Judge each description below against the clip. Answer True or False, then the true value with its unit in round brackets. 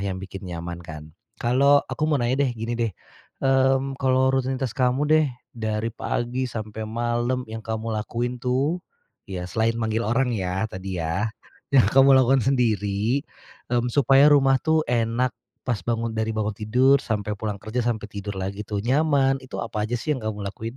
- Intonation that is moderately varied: True (3.7 semitones)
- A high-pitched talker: False (115 Hz)